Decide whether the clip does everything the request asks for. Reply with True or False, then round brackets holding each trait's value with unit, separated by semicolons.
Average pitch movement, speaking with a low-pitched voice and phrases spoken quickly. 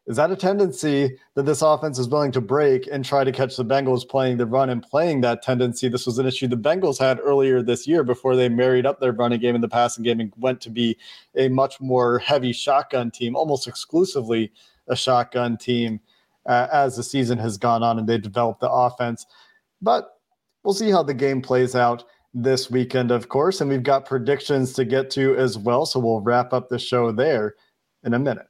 False (2.1 semitones; 125 Hz; 215 wpm)